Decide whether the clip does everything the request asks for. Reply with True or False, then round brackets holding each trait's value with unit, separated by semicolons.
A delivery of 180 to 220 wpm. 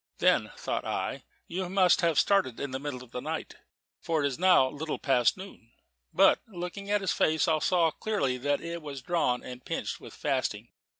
True (195 wpm)